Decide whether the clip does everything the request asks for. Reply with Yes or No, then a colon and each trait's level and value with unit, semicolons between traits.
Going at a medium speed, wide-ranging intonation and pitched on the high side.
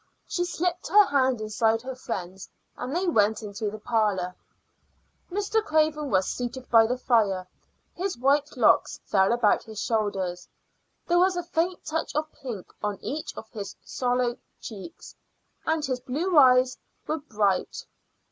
Yes: average, 150 wpm; wide, 6.6 semitones; very high, 250 Hz